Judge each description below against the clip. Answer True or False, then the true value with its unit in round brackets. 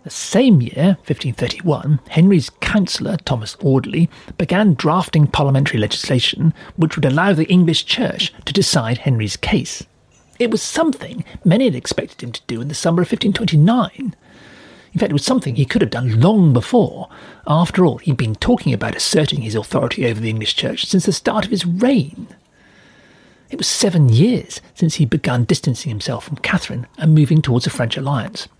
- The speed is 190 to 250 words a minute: False (175 wpm)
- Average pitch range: False (6.5 semitones)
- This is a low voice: False (155 Hz)